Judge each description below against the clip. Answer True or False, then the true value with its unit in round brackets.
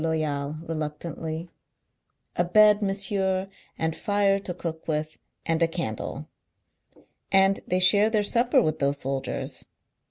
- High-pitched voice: False (170 Hz)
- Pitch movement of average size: True (3.9 semitones)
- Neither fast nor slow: False (115 wpm)